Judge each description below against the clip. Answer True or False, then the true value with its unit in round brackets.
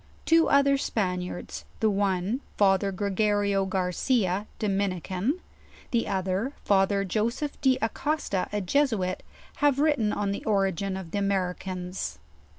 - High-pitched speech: True (200 Hz)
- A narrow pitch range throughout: False (3.5 semitones)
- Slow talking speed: True (130 wpm)